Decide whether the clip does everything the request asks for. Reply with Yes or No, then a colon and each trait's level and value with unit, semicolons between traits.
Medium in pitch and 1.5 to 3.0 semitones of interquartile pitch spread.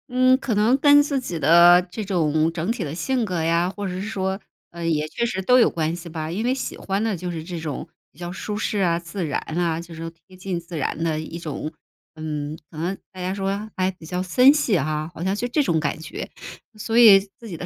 No: medium, 180 Hz; average, 4.2 semitones